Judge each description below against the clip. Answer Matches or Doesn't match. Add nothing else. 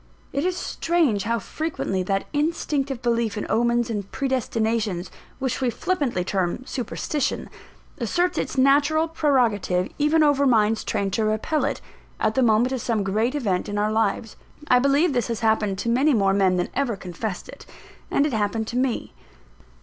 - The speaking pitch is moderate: Doesn't match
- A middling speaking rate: Matches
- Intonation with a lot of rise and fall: Doesn't match